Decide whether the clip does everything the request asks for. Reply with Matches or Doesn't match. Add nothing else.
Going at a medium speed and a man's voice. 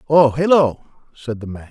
Matches